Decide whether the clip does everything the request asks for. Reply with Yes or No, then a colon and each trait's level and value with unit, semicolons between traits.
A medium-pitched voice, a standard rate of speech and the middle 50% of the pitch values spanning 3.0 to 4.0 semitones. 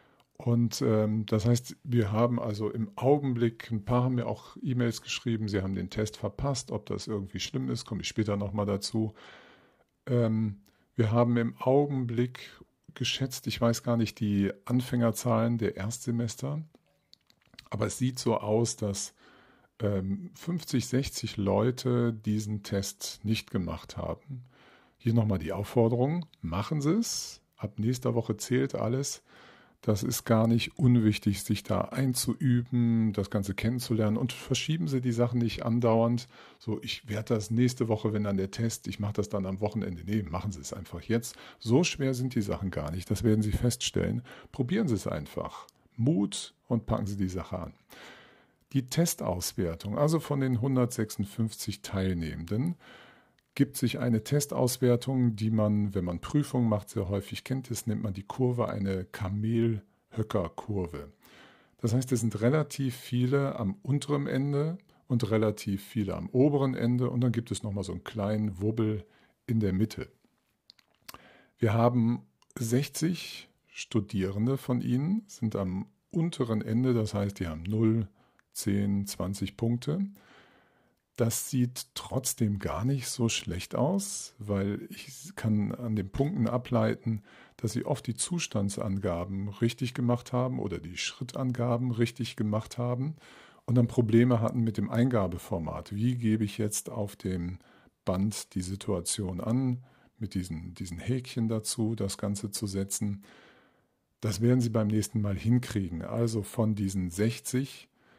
No: low, 115 Hz; average, 150 wpm; average, 3.4 semitones